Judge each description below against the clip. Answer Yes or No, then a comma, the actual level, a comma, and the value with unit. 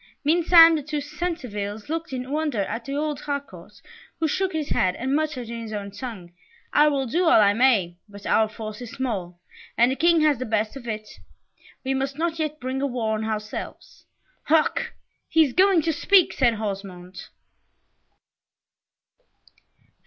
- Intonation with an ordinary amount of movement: No, wide, 6.1 semitones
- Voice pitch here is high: Yes, very high, 260 Hz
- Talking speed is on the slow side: No, average, 170 wpm